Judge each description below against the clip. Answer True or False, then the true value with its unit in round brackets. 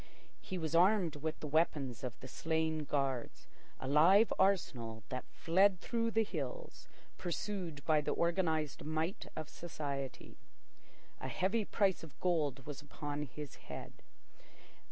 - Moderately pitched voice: True (160 Hz)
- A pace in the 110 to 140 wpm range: True (135 wpm)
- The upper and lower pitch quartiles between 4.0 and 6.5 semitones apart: True (4.3 semitones)